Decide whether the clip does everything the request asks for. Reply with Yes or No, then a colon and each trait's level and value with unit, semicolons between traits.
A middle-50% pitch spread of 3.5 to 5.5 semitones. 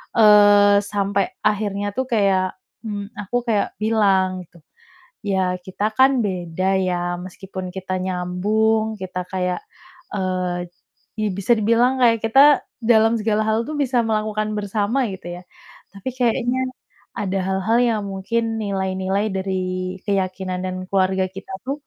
No: average, 2.9 semitones